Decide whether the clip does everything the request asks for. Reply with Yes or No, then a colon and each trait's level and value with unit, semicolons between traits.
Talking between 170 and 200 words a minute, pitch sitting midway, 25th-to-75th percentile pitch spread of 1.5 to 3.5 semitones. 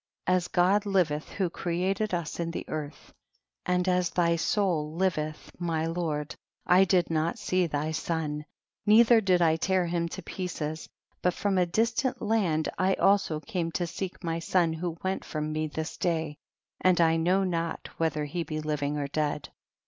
Yes: average, 180 wpm; medium, 170 Hz; average, 2.9 semitones